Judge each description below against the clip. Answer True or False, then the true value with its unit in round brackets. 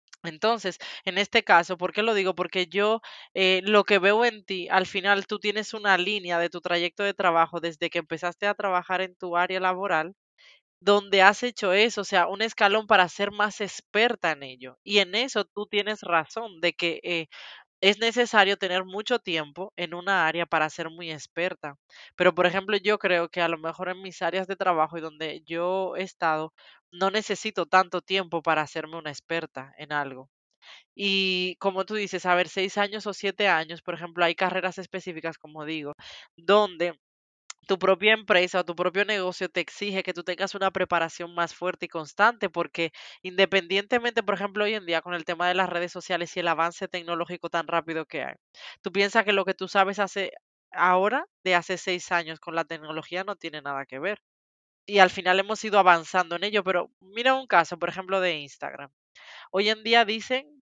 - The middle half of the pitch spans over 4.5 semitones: False (2.9 semitones)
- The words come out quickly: True (200 wpm)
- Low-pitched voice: False (185 Hz)